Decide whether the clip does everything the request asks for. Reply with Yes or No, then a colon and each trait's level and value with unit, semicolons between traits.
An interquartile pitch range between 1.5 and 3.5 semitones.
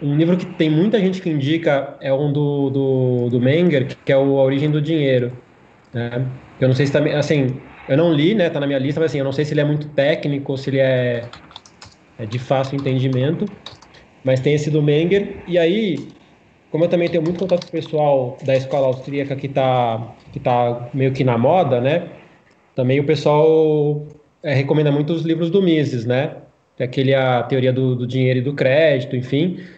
Yes: average, 3.1 semitones